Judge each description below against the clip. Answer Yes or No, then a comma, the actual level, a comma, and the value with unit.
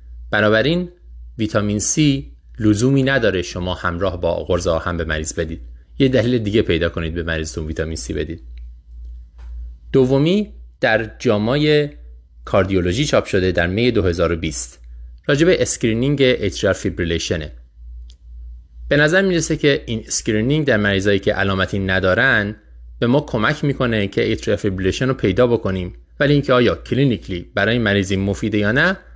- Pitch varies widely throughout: Yes, wide, 7.8 semitones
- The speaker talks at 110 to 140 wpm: Yes, average, 135 wpm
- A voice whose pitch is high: No, very low, 95 Hz